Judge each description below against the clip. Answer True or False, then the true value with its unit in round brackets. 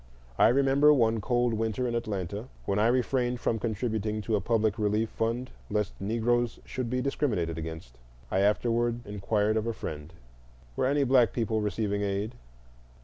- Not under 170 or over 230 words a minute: False (160 wpm)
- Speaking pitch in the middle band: False (110 Hz)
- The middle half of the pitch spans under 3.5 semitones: True (2.9 semitones)